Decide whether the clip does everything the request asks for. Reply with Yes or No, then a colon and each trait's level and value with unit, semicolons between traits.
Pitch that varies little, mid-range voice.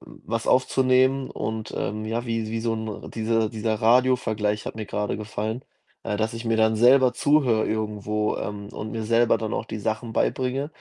No: narrow, 1.9 semitones; low, 110 Hz